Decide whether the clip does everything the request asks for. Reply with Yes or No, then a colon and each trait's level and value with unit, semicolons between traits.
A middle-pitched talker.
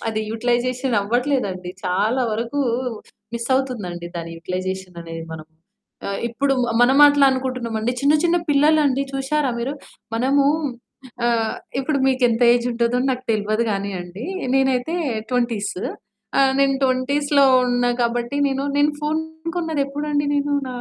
No: very high, 250 Hz